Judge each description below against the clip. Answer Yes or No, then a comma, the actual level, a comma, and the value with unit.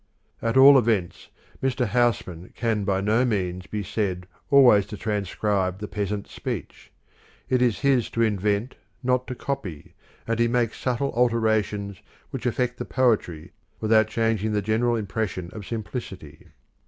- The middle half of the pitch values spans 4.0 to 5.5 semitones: No, average, 3.3 semitones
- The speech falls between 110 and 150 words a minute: Yes, average, 145 wpm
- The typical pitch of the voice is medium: No, low, 110 Hz